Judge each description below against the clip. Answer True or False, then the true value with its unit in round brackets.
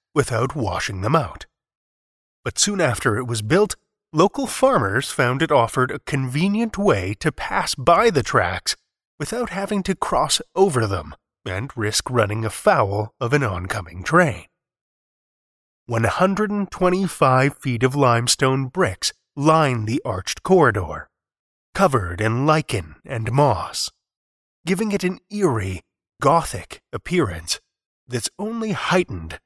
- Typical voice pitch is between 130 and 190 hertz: True (135 Hz)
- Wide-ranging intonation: True (8.9 semitones)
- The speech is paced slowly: True (120 wpm)